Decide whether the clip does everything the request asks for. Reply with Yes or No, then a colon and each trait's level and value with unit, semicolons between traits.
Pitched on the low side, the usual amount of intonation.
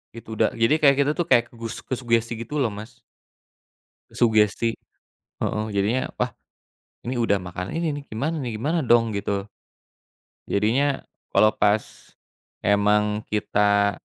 Yes: low, 115 Hz; average, 3.1 semitones